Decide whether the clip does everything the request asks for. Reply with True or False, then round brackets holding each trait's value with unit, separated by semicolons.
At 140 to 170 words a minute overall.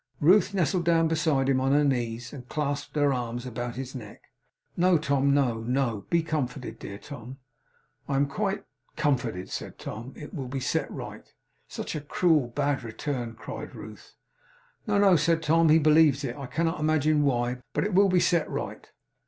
False (180 wpm)